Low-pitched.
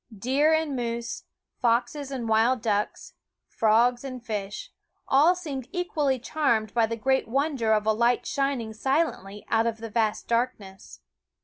No: high, 240 Hz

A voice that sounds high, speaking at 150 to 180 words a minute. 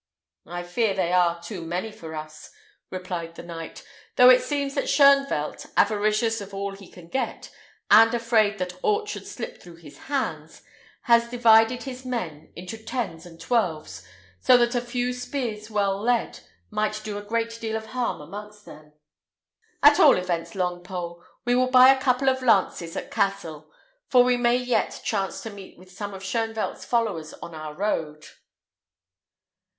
Yes: high, 210 Hz; average, 165 wpm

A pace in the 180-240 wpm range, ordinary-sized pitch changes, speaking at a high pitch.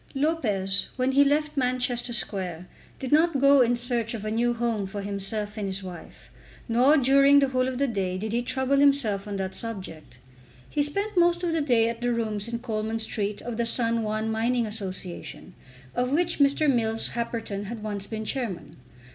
Yes: average, 190 wpm; average, 4.2 semitones; high, 235 Hz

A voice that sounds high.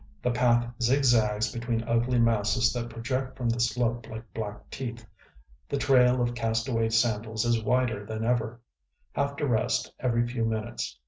No: low, 120 Hz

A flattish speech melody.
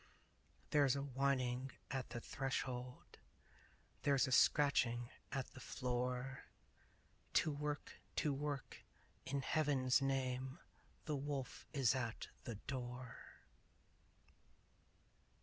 Yes: narrow, 1.9 semitones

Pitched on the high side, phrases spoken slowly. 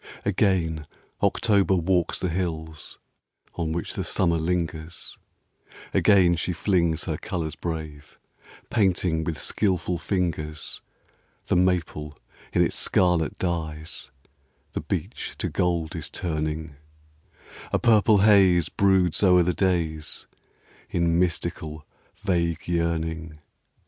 No: very low, 85 Hz; slow, 110 wpm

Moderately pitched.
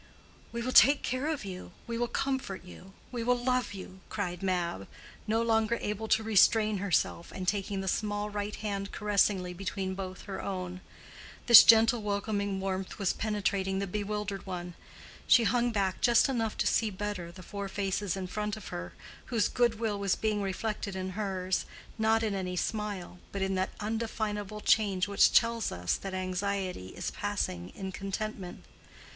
No: high, 200 Hz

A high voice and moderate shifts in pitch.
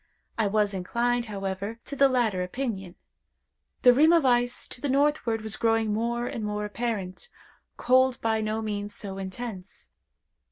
Yes: high, 225 Hz; average, 3.1 semitones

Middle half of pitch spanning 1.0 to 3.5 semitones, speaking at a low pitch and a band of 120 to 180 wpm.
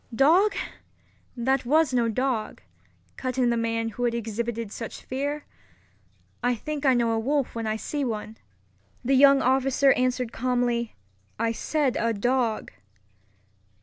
No: average, 2.8 semitones; high, 245 Hz; average, 145 wpm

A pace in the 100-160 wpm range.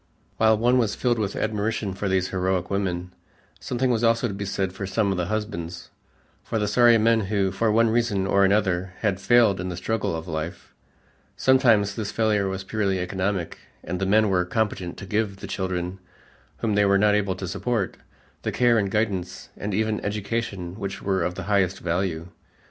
No: average, 195 wpm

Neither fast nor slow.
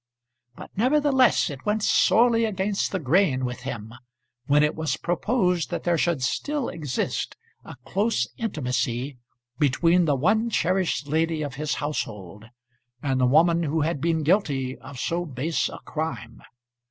Yes: average, 150 wpm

